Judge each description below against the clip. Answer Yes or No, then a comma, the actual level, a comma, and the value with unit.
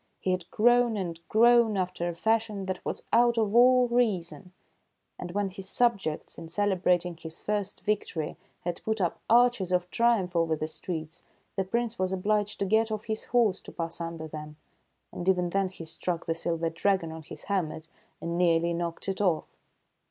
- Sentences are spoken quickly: No, average, 180 wpm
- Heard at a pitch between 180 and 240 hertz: Yes, medium, 185 Hz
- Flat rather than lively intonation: No, average, 4.2 semitones